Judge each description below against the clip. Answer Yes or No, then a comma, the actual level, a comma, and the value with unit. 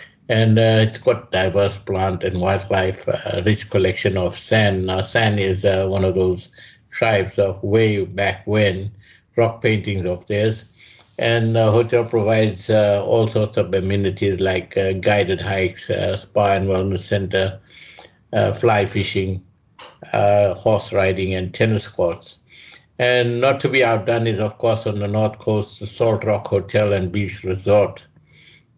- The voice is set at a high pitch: No, low, 100 Hz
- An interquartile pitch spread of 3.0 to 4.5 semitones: No, narrow, 2.4 semitones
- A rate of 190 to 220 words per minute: No, average, 155 wpm